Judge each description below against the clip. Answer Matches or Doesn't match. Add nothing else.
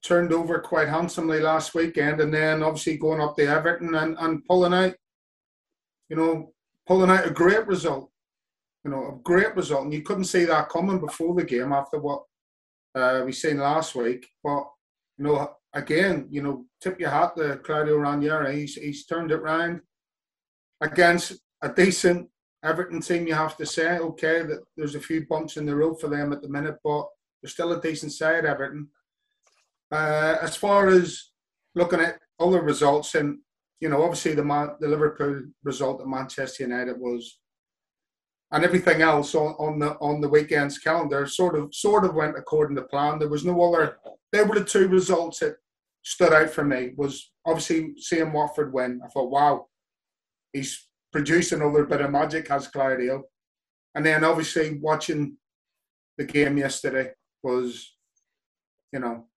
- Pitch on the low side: Doesn't match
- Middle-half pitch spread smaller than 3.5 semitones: Matches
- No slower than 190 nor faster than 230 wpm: Doesn't match